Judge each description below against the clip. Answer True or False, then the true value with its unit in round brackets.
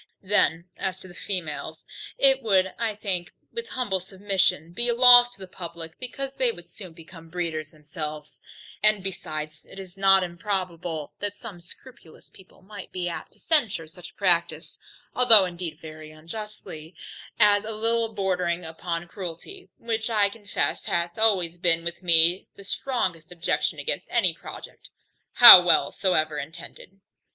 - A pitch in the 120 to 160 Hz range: False (185 Hz)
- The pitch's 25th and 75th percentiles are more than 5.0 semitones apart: False (4.0 semitones)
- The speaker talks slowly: False (155 wpm)